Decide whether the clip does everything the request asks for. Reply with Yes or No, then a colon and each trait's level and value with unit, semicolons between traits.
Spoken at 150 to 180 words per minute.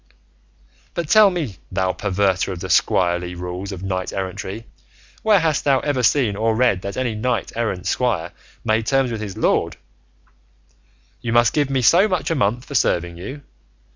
Yes: average, 170 wpm